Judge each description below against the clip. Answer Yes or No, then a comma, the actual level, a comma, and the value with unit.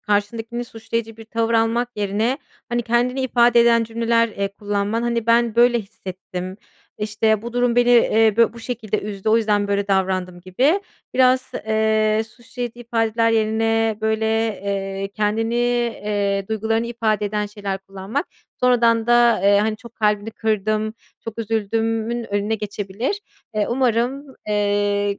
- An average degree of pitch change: No, narrow, 2.3 semitones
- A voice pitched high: Yes, high, 220 Hz